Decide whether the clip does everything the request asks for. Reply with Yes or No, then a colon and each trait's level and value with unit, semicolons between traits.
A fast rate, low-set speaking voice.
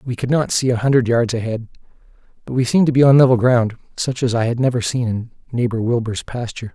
Yes: fast, 230 wpm; low, 120 Hz